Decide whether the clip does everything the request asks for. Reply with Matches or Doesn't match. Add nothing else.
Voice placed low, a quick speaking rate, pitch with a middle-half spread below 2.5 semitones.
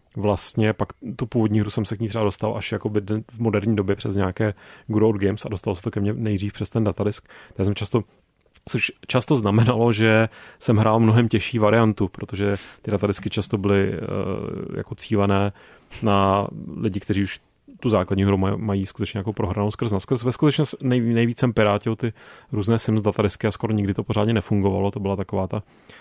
Matches